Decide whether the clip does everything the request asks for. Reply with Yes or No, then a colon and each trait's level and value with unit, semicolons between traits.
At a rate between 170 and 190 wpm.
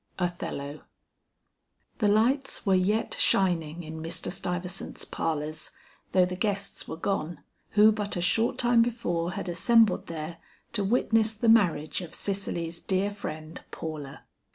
No: slow, 135 wpm